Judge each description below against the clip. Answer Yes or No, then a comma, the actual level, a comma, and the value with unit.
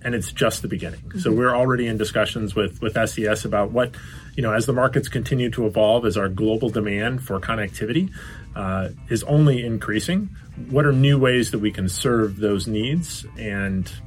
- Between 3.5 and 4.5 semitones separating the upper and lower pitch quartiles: No, average, 2.9 semitones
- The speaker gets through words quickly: No, average, 190 wpm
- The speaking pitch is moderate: No, low, 110 Hz